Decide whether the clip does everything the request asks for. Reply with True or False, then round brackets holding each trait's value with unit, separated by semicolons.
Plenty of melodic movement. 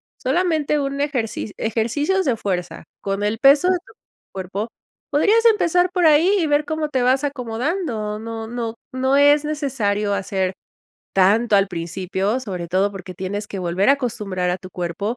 True (6.7 semitones)